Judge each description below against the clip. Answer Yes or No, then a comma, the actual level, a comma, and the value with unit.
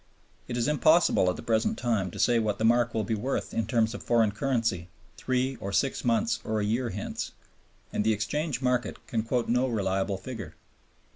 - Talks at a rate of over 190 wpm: Yes, average, 200 wpm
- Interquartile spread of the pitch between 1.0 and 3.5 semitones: Yes, average, 2.9 semitones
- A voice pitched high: No, low, 115 Hz